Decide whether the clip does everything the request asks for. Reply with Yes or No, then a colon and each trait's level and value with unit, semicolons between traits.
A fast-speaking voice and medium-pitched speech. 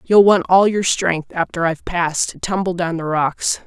Yes: fast, 215 wpm; medium, 175 Hz